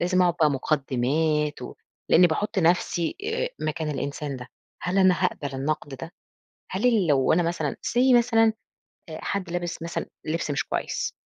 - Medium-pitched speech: Yes, medium, 165 Hz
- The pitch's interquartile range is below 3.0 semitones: No, average, 4.0 semitones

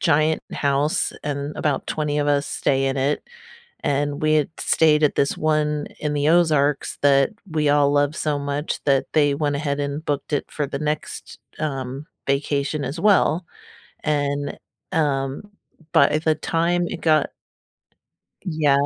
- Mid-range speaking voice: Yes, medium, 145 Hz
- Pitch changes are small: Yes, narrow, 1.5 semitones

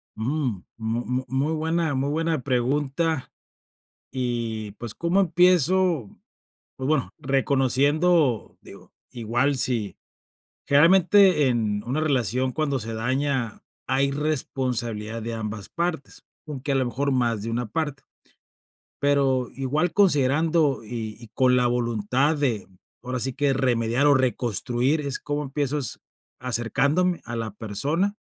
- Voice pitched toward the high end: No, low, 130 Hz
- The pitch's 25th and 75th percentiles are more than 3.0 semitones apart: Yes, average, 4.0 semitones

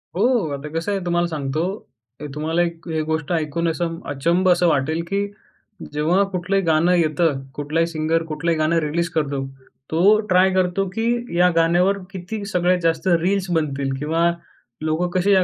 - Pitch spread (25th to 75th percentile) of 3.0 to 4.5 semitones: No, narrow, 2.5 semitones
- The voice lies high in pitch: No, medium, 170 Hz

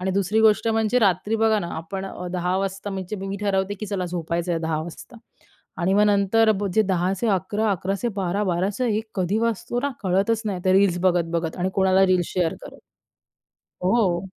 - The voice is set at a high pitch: Yes, high, 195 Hz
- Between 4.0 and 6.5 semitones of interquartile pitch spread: No, average, 2.8 semitones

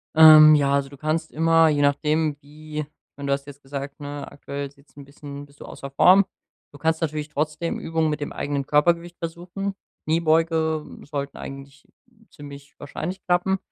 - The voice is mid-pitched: Yes, medium, 150 Hz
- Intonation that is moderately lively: No, narrow, 2.3 semitones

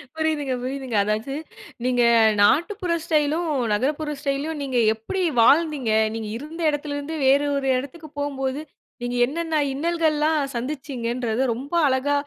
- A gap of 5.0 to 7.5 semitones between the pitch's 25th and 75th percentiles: No, average, 3.3 semitones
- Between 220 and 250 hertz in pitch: No, very high, 285 Hz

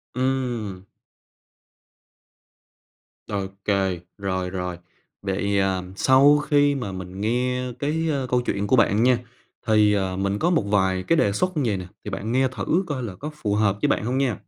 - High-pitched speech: No, low, 105 Hz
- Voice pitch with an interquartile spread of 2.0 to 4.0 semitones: No, average, 5.3 semitones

